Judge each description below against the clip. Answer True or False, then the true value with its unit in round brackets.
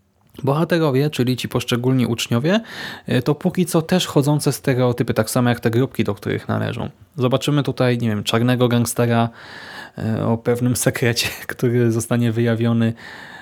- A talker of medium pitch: False (125 Hz)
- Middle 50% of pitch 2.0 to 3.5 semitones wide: True (2.8 semitones)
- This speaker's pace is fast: False (140 wpm)